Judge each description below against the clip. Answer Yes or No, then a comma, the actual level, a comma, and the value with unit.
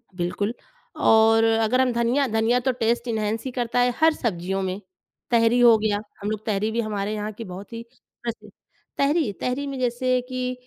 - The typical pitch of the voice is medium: No, high, 230 Hz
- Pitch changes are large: No, average, 2.7 semitones